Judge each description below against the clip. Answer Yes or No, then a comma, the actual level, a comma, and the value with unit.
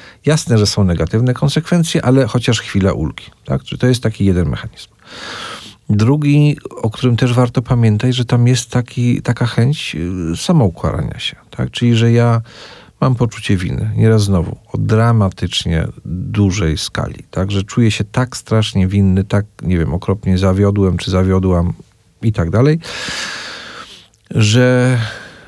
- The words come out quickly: No, average, 140 wpm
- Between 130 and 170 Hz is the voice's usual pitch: No, low, 110 Hz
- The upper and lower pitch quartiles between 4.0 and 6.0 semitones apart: Yes, average, 4.7 semitones